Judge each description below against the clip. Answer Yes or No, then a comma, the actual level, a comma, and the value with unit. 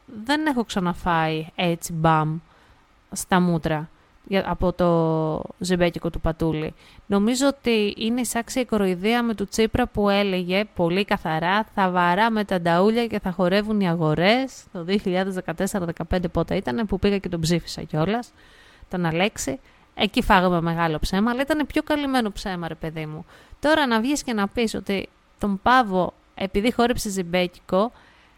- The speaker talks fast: No, average, 150 wpm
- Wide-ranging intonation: No, average, 4.7 semitones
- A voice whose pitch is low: No, high, 195 Hz